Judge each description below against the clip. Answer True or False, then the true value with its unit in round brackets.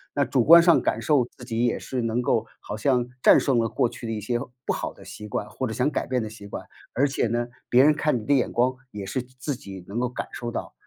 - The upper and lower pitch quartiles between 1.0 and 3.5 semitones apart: True (2.7 semitones)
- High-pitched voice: False (125 Hz)